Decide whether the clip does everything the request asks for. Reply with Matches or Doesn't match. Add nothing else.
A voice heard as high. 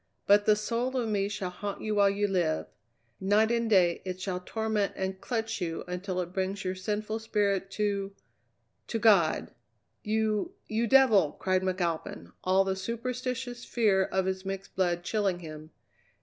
Matches